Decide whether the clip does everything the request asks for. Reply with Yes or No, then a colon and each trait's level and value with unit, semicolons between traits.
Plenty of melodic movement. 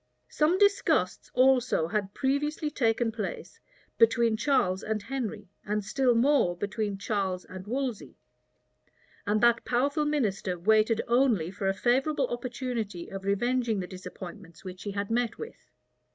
No: average, 4.6 semitones